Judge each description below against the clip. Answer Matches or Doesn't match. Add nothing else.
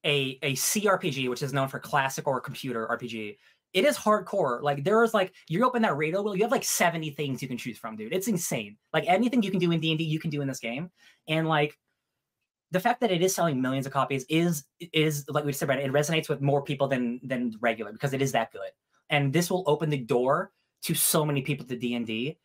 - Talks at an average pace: Doesn't match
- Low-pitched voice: Doesn't match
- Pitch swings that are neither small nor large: Matches